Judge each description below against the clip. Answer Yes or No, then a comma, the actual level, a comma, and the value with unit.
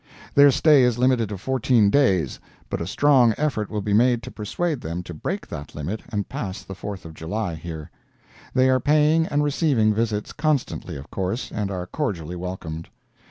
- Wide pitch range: Yes, wide, 6.5 semitones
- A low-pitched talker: Yes, low, 110 Hz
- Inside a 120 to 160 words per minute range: No, average, 185 wpm